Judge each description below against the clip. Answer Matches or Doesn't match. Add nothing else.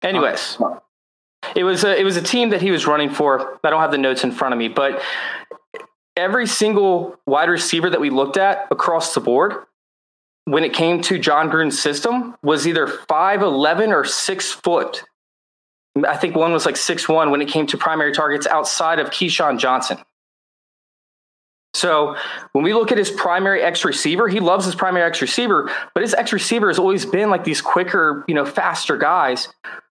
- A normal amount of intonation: Matches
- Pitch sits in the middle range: Matches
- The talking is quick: Doesn't match